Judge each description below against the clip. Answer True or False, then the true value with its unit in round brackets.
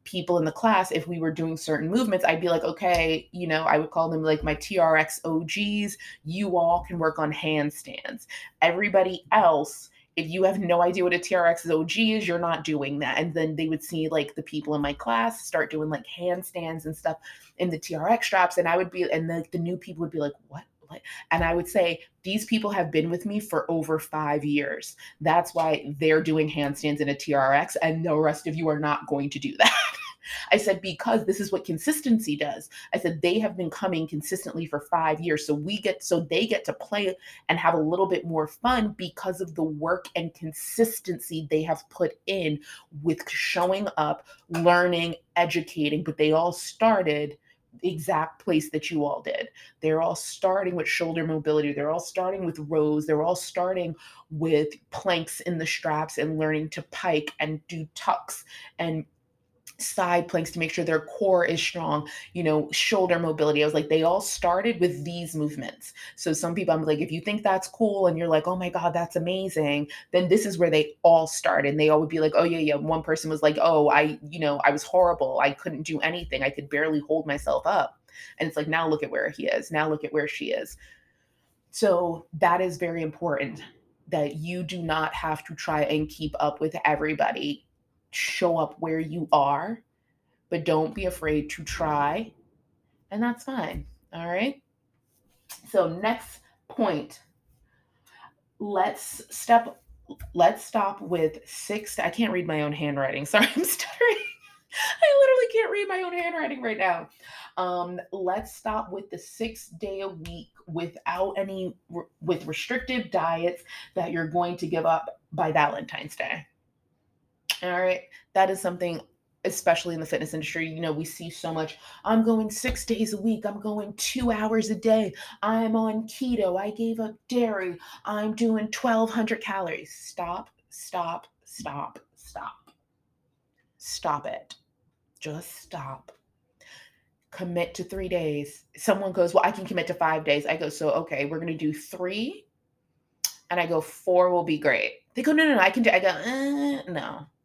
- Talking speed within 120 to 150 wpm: False (190 wpm)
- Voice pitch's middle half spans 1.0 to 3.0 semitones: False (3.5 semitones)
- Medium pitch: True (170 Hz)